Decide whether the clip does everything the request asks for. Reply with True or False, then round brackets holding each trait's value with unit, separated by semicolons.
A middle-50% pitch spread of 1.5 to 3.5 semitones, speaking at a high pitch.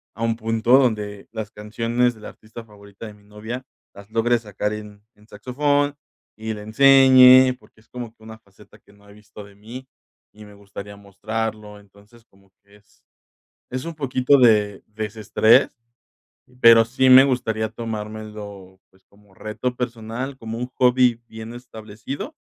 False (2.9 semitones; 110 Hz)